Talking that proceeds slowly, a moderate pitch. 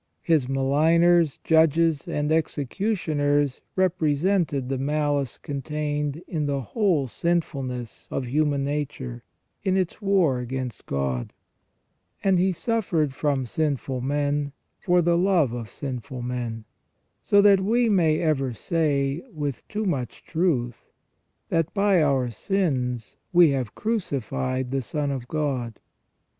Yes: slow, 125 wpm; medium, 145 Hz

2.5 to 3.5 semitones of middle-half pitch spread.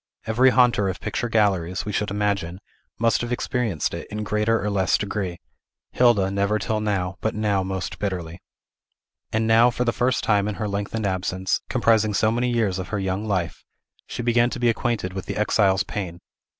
Yes: average, 3.1 semitones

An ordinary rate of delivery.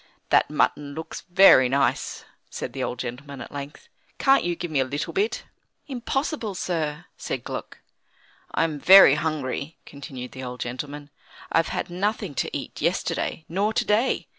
Yes: average, 160 wpm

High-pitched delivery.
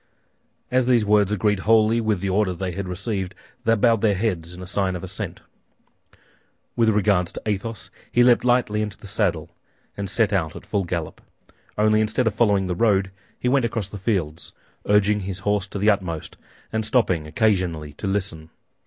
No: low, 100 Hz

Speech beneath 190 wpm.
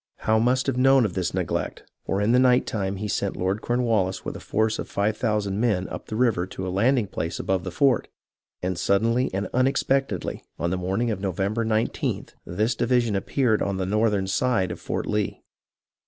No: average, 200 wpm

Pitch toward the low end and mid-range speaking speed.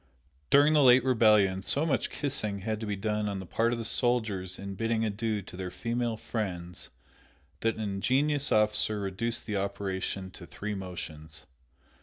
Yes: low, 105 Hz; average, 170 wpm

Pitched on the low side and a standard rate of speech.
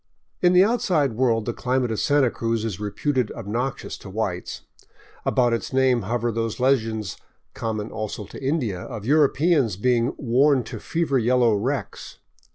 Yes: low, 120 Hz; average, 155 wpm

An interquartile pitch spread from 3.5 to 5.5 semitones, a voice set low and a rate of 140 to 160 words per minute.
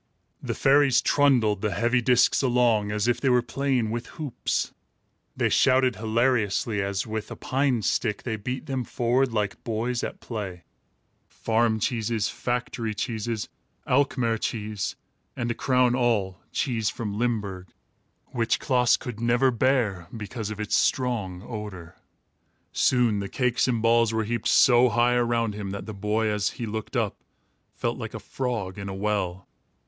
No: average, 2.8 semitones; low, 115 Hz; average, 155 wpm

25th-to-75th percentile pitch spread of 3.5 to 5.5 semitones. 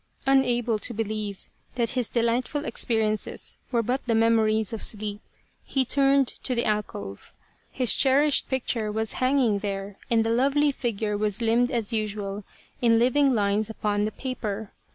No: average, 3.1 semitones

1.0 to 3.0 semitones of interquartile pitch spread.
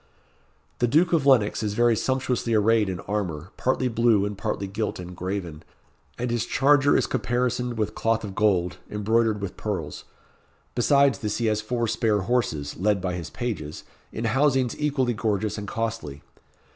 No: average, 3.6 semitones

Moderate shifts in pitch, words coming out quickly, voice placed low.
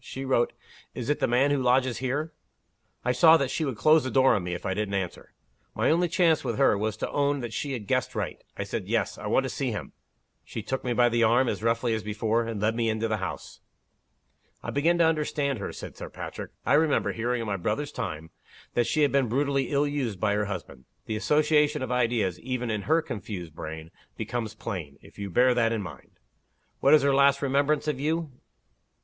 Yes: average, 4.8 semitones; fast, 225 wpm; low, 125 Hz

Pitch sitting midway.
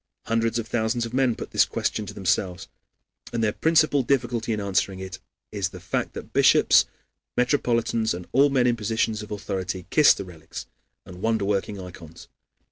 No: low, 110 Hz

